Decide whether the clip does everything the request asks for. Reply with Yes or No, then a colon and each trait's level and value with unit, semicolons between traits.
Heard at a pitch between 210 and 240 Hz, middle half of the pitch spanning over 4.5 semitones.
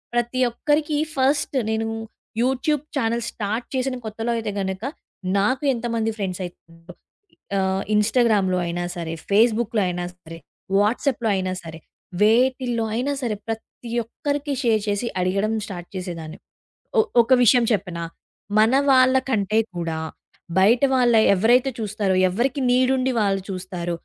Yes: high, 220 Hz; average, 4.9 semitones